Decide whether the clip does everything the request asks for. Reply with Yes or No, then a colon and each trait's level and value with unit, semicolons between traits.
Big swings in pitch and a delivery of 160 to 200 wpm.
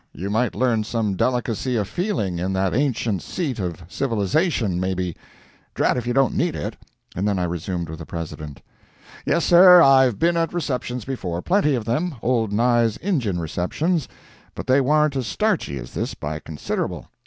Yes: wide, 7.1 semitones; average, 170 wpm